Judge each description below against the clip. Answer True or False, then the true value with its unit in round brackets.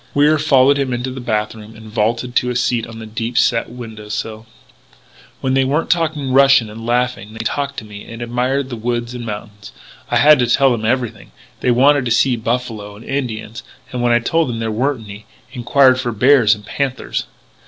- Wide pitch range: False (3.0 semitones)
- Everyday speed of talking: False (210 wpm)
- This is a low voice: True (120 Hz)